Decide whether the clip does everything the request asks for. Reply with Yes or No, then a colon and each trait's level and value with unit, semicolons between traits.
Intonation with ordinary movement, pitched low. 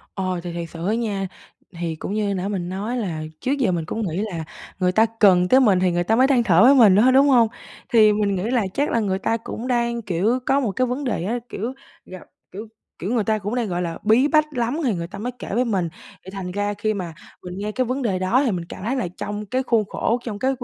No: average, 4.6 semitones; high, 210 Hz